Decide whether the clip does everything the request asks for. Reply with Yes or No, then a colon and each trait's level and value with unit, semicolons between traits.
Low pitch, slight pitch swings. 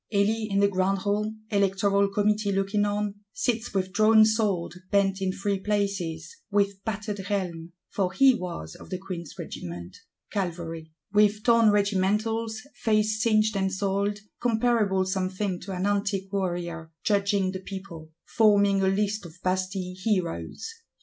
No: high, 200 Hz; narrow, 2.1 semitones